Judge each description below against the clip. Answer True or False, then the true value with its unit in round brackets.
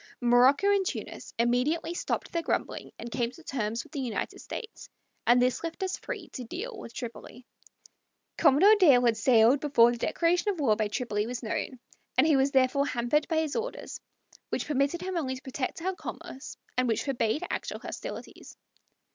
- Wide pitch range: True (5.7 semitones)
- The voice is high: True (270 Hz)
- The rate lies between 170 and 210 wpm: True (180 wpm)